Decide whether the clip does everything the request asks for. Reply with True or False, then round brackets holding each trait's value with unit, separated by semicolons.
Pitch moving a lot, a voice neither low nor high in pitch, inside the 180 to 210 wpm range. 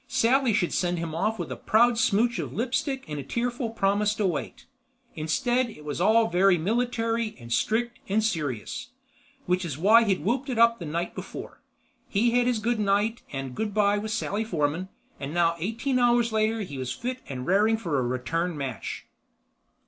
False (5.7 semitones; 215 Hz; 185 wpm)